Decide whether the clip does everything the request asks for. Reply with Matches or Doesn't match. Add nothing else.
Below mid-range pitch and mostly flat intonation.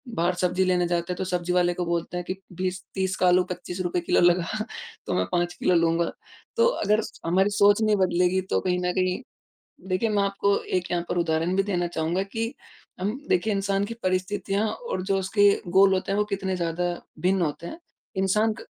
Doesn't match